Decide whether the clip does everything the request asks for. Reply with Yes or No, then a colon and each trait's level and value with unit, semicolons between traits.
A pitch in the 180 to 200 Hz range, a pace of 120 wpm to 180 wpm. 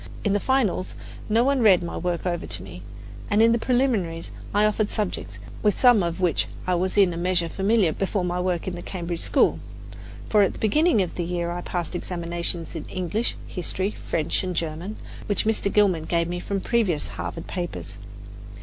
No: medium, 185 Hz; average, 195 wpm